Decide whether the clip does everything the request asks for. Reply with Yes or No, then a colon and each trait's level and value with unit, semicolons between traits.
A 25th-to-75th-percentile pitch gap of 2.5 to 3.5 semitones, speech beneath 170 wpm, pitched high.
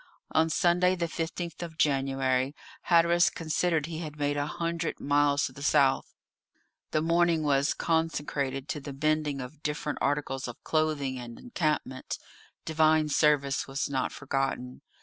No: average, 2.9 semitones; average, 145 wpm; medium, 150 Hz